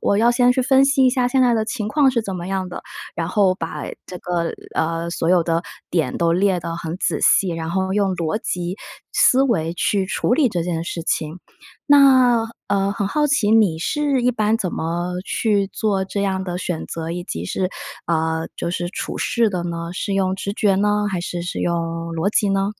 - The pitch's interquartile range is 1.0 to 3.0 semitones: No, average, 4.5 semitones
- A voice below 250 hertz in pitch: Yes, high, 190 Hz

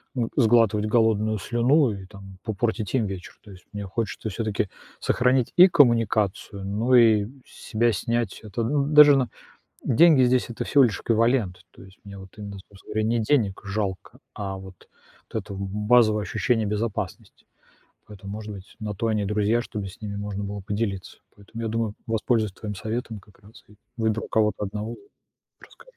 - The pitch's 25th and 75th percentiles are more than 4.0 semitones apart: No, narrow, 2.6 semitones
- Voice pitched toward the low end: Yes, low, 110 Hz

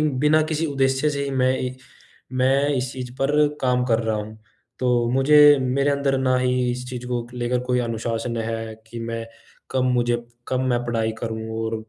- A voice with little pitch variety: Yes, narrow, 2.3 semitones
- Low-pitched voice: Yes, low, 125 Hz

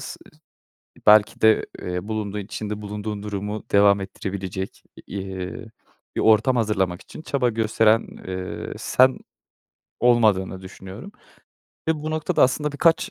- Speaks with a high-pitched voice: No, low, 105 Hz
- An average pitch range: Yes, average, 3.5 semitones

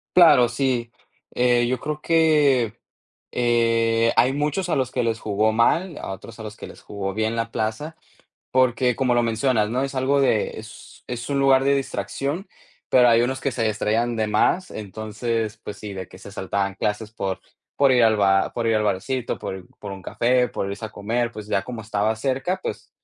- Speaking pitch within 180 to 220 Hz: No, low, 115 Hz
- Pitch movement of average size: Yes, average, 3.4 semitones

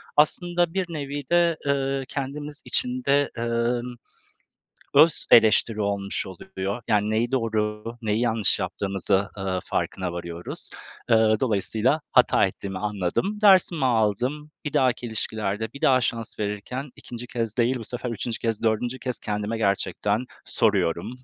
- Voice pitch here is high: No, low, 115 Hz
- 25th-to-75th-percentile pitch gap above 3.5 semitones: Yes, average, 4.4 semitones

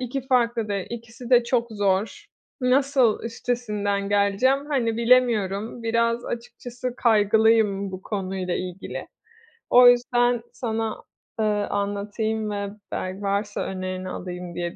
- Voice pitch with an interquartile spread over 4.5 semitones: No, average, 3.2 semitones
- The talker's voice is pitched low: No, high, 220 Hz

